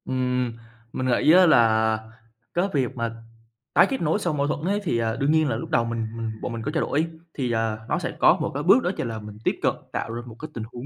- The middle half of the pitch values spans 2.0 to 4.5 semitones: No, wide, 5.4 semitones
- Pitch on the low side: Yes, low, 125 Hz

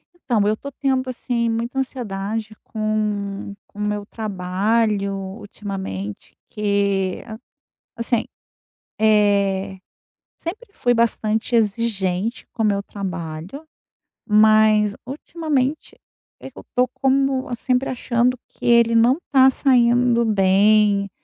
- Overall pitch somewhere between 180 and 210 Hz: No, high, 220 Hz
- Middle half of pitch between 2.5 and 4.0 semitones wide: Yes, average, 3.6 semitones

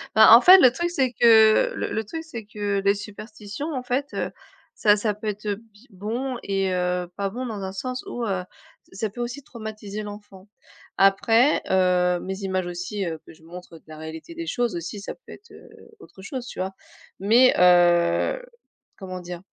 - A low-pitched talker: No, high, 205 Hz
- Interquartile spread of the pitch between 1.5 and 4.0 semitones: No, average, 4.5 semitones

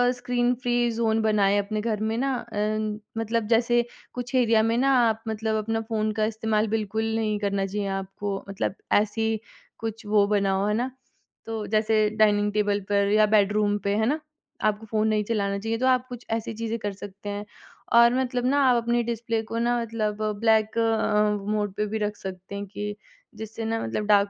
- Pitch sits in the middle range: No, high, 215 Hz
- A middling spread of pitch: No, narrow, 1.7 semitones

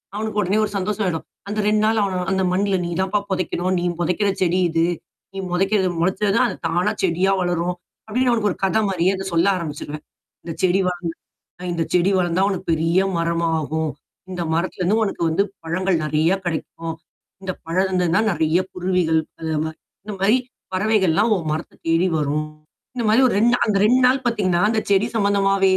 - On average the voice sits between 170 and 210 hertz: Yes, medium, 185 Hz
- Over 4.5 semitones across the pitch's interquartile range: No, average, 3.3 semitones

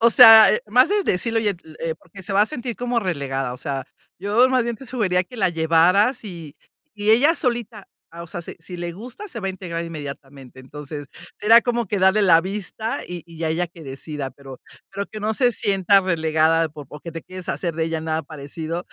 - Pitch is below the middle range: No, medium, 180 Hz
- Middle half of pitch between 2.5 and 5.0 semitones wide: No, wide, 5.4 semitones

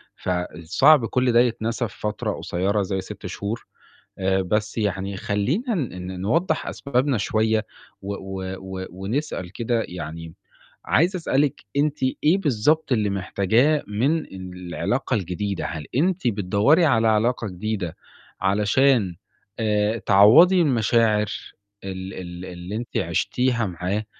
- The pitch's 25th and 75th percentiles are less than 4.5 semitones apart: No, average, 5.0 semitones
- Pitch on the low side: Yes, low, 105 Hz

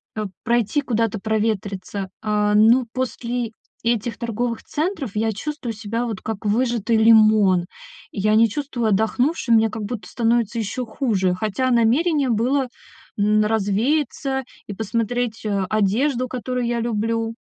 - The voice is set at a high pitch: Yes, high, 225 Hz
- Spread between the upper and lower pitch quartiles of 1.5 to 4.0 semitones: Yes, narrow, 2.5 semitones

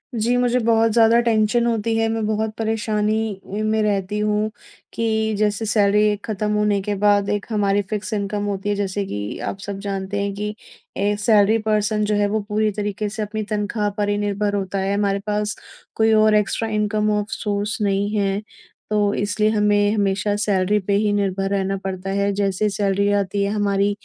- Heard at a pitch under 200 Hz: No, high, 205 Hz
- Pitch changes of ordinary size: No, narrow, 1.2 semitones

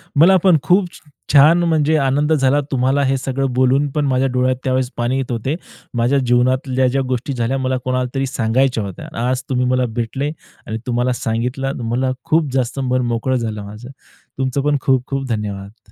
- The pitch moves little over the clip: Yes, narrow, 2.0 semitones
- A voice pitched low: Yes, low, 130 Hz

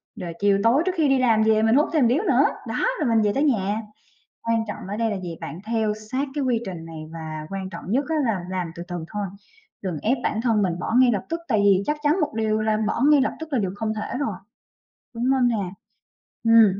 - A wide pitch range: No, average, 4.7 semitones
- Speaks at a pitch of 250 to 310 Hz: No, high, 220 Hz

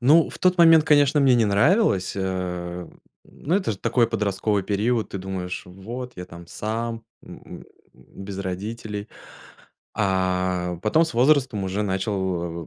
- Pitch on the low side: Yes, low, 100 Hz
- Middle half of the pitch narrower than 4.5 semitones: No, average, 4.9 semitones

